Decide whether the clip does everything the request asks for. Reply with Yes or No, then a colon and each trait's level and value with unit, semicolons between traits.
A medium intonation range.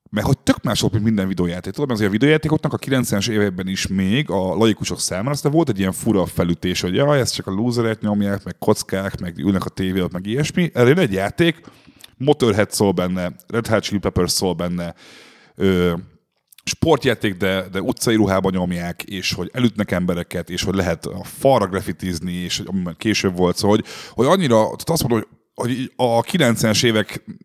Yes: average, 4.9 semitones